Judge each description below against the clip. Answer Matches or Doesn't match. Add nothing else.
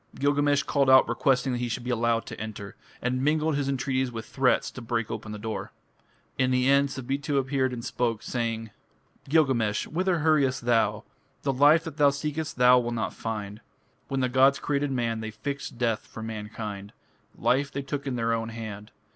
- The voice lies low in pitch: Matches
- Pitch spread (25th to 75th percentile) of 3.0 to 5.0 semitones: Matches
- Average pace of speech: Matches